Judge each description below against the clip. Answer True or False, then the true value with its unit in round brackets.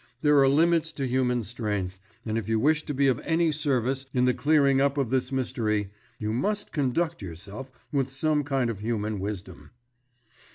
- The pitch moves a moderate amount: True (4.8 semitones)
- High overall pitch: False (130 Hz)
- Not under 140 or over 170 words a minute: False (180 wpm)